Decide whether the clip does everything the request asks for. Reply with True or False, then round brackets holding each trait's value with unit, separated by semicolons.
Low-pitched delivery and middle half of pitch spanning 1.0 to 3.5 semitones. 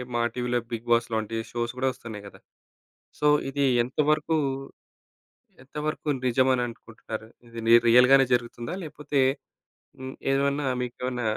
True (125 Hz; 3.0 semitones)